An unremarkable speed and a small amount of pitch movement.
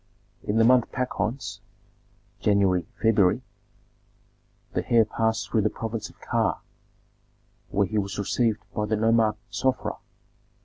No: slow, 125 wpm; narrow, 1.9 semitones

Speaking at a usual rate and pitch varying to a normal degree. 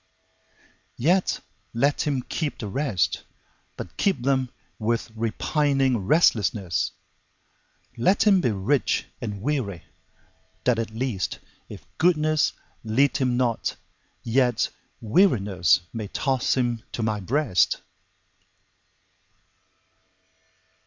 No: slow, 85 wpm; average, 4.8 semitones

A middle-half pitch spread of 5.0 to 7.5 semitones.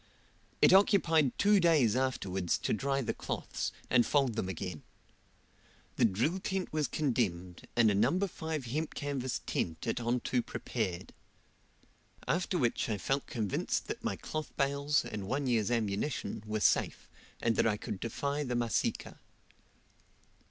Yes: wide, 5.6 semitones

